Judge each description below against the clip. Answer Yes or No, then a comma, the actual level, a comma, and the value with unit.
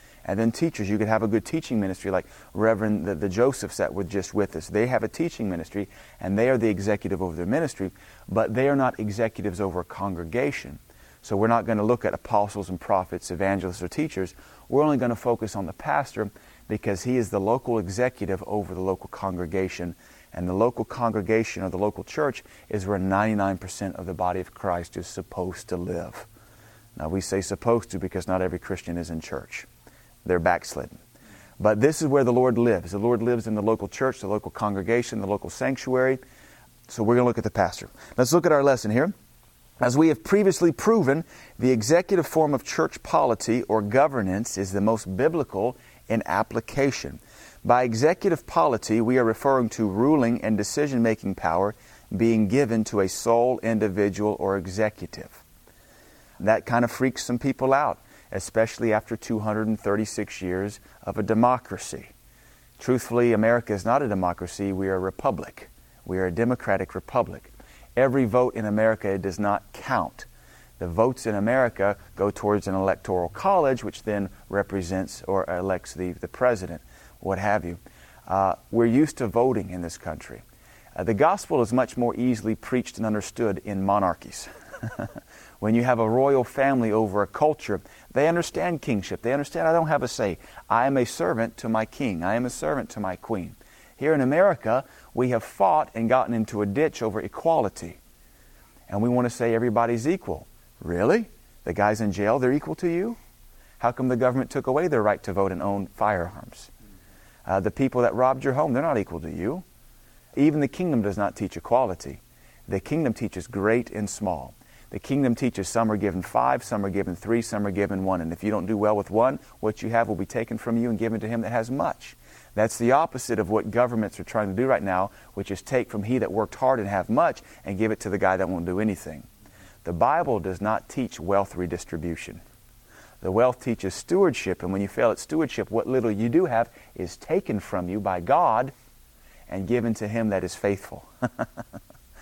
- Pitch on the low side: Yes, low, 110 Hz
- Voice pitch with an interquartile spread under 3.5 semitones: No, average, 3.8 semitones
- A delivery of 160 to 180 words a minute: No, average, 195 wpm